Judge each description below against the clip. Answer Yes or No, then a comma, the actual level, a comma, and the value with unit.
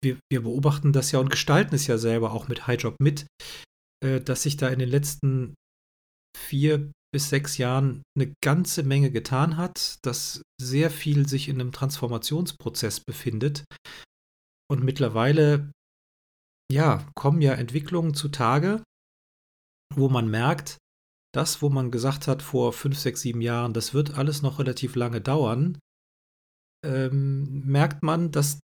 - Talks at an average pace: Yes, average, 140 wpm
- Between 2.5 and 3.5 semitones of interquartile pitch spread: Yes, average, 2.9 semitones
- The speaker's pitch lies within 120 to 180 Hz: Yes, medium, 140 Hz